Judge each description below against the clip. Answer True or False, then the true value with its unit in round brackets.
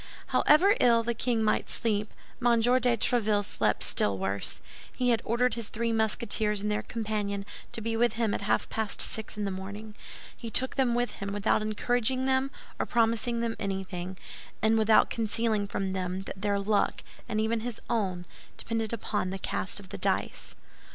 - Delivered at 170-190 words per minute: True (180 wpm)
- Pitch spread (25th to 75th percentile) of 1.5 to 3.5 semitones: True (2.6 semitones)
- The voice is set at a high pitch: True (220 Hz)